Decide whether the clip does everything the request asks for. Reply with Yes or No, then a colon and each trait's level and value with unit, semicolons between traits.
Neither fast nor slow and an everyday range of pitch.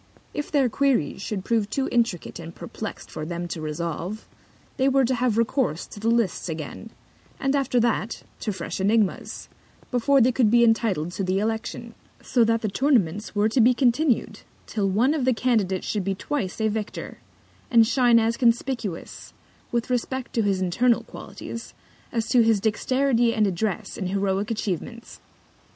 Yes: average, 170 wpm; average, 3.9 semitones